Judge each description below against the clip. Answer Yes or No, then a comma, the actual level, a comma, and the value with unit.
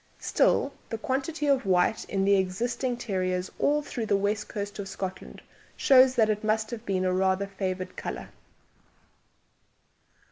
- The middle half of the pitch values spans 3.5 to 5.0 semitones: Yes, average, 4.3 semitones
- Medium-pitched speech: No, high, 205 Hz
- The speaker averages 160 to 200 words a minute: No, average, 150 wpm